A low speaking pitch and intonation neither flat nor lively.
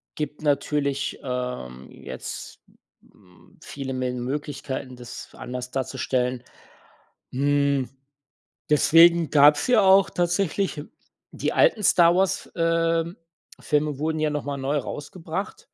No: medium, 145 Hz; average, 4.1 semitones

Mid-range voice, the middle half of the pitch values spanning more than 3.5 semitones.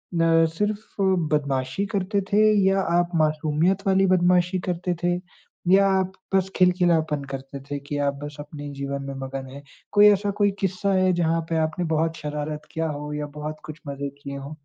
Yes: medium, 165 Hz; average, 4.2 semitones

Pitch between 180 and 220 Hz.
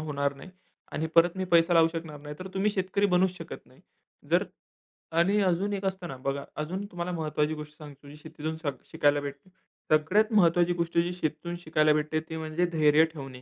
No: medium, 160 Hz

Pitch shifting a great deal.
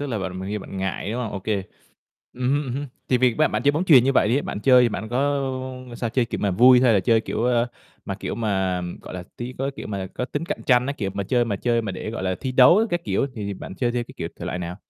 No: average, 4.4 semitones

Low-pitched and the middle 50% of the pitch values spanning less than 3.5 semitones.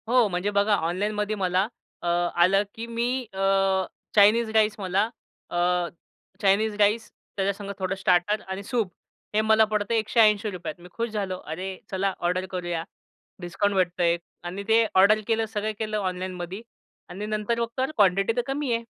No: high, 200 Hz; average, 2.8 semitones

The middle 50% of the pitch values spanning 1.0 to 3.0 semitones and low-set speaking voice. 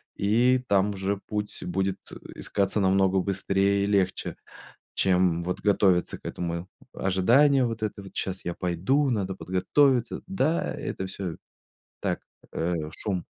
Yes: narrow, 2.4 semitones; very low, 95 Hz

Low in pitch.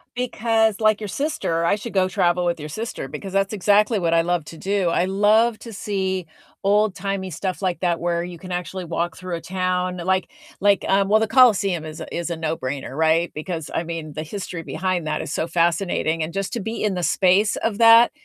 No: medium, 185 Hz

